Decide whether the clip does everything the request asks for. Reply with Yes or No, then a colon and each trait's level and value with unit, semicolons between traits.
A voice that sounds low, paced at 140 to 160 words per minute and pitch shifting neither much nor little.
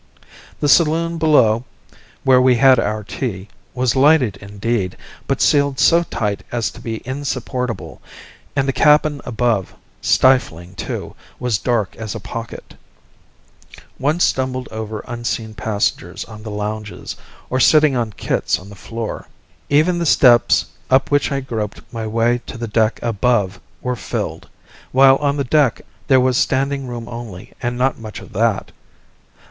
Yes: low, 120 Hz; average, 150 wpm; average, 3.8 semitones